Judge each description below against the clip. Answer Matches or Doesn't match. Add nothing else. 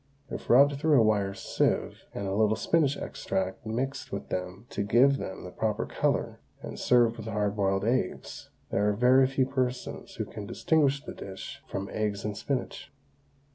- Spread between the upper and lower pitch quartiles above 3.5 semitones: Matches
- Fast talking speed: Doesn't match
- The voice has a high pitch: Doesn't match